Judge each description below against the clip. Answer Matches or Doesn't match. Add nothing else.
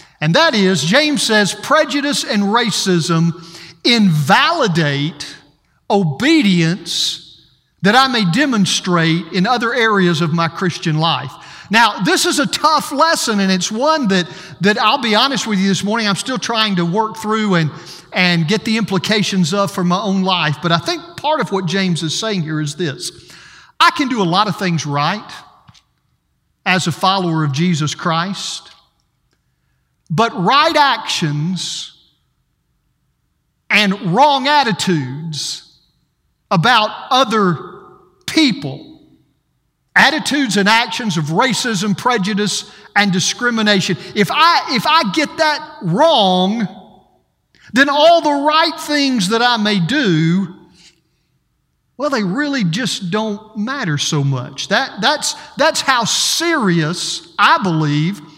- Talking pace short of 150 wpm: Matches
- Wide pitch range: Matches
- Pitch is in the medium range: Doesn't match